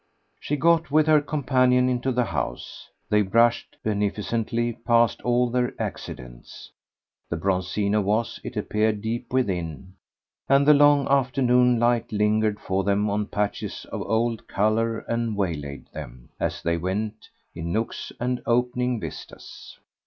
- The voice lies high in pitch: No, low, 115 Hz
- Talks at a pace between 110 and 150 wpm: Yes, average, 140 wpm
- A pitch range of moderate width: Yes, average, 3.5 semitones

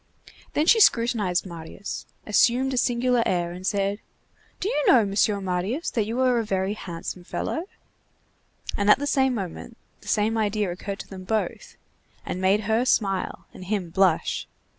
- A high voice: Yes, high, 210 Hz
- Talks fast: No, average, 165 wpm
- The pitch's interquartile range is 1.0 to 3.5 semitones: No, average, 4.1 semitones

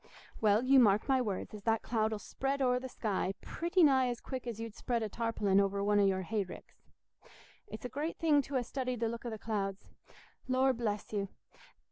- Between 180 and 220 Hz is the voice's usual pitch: No, high, 230 Hz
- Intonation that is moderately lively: Yes, average, 3.8 semitones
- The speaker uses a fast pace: Yes, fast, 215 wpm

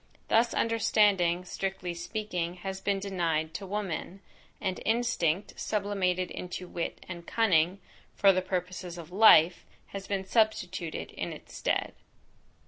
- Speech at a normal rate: No, slow, 130 wpm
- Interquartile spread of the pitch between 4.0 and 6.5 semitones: No, narrow, 2.5 semitones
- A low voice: No, medium, 185 Hz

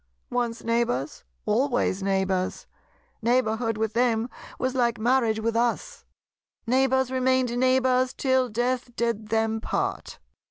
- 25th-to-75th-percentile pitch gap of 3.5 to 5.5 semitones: No, narrow, 2.5 semitones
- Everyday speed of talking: No, slow, 115 wpm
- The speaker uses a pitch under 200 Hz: No, high, 235 Hz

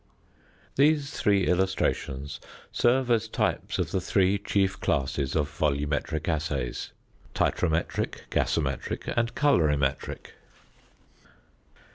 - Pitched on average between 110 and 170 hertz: No, very low, 90 Hz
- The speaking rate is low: Yes, slow, 90 wpm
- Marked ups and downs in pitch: Yes, wide, 6.3 semitones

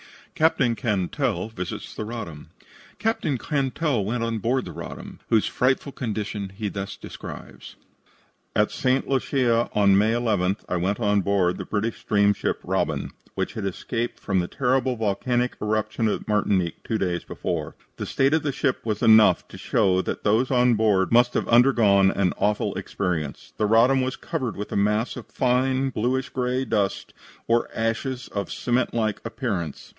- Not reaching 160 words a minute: No, average, 165 wpm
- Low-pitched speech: Yes, low, 115 Hz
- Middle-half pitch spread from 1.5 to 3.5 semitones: No, average, 3.9 semitones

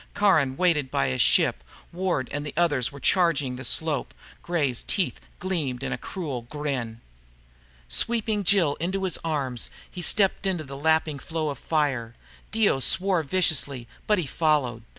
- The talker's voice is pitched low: No, medium, 150 Hz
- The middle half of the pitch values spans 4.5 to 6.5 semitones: Yes, average, 5.3 semitones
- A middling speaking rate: Yes, average, 155 wpm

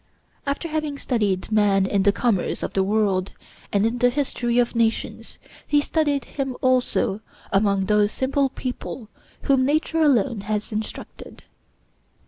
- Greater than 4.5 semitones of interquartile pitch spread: Yes, average, 4.9 semitones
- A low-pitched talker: No, high, 235 Hz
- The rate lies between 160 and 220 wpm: No, average, 140 wpm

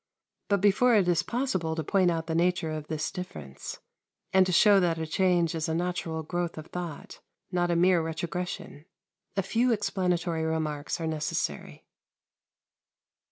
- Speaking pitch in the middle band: Yes, medium, 175 Hz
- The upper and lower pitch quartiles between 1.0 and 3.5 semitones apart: Yes, narrow, 2.4 semitones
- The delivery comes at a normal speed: Yes, average, 160 wpm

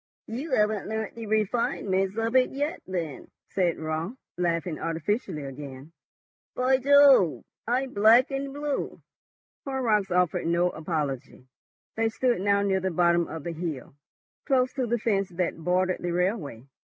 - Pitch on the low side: No, high, 195 Hz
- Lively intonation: Yes, wide, 6.1 semitones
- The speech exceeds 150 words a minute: No, average, 145 wpm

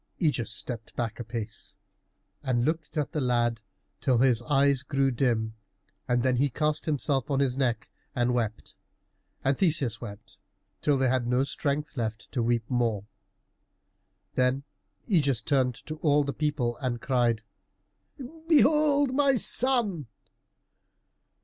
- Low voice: Yes, low, 130 Hz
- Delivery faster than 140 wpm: No, slow, 135 wpm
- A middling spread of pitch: Yes, average, 3.9 semitones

